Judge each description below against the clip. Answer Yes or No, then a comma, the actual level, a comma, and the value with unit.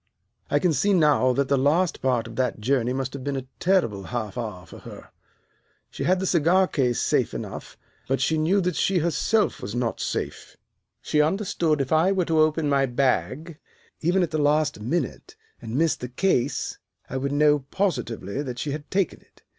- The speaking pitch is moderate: Yes, medium, 145 Hz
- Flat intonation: No, average, 5.0 semitones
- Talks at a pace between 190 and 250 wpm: Yes, average, 195 wpm